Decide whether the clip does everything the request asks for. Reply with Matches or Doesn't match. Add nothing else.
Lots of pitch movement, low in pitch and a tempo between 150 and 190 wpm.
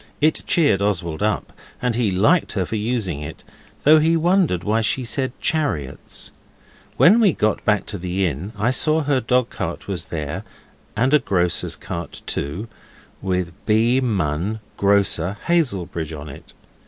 Matches